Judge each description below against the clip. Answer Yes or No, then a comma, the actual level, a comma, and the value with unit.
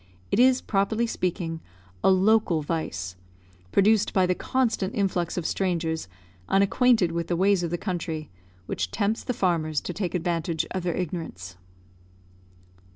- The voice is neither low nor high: Yes, medium, 180 Hz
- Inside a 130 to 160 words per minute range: Yes, average, 145 wpm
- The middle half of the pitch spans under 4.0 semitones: Yes, average, 3.4 semitones